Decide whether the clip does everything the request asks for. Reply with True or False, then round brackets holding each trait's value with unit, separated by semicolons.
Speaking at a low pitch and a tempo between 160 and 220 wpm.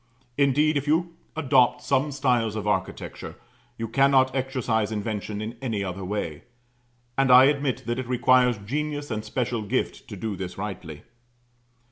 False (125 Hz; 150 wpm)